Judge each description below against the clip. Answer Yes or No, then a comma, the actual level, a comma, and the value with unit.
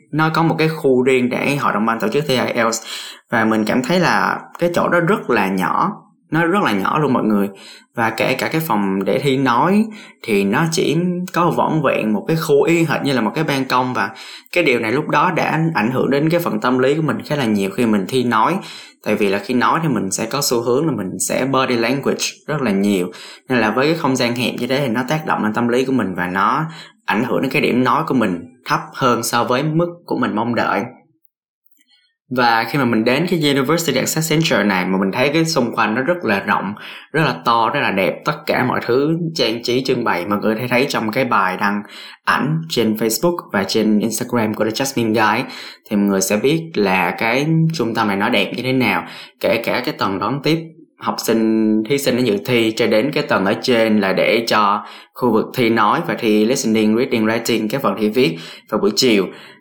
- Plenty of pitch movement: Yes, wide, 6.2 semitones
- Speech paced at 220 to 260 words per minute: Yes, average, 245 wpm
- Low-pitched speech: Yes, low, 125 Hz